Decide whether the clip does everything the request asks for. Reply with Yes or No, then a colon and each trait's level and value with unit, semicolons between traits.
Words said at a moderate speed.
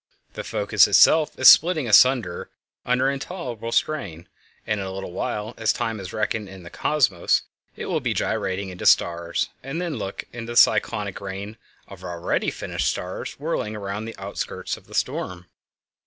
Yes: average, 170 wpm